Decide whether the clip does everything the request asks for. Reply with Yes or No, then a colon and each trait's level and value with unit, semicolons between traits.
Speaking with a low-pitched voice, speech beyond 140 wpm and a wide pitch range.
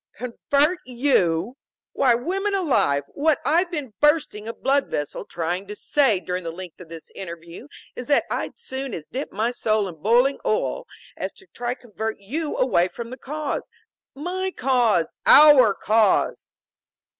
No: high, 245 Hz; average, 155 wpm; wide, 7.0 semitones